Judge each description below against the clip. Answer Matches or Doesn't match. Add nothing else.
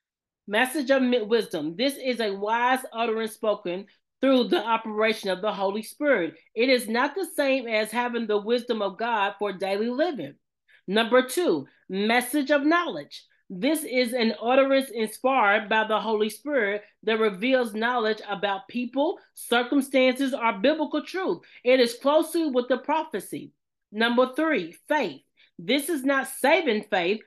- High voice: Matches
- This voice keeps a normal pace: Matches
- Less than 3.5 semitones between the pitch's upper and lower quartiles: Doesn't match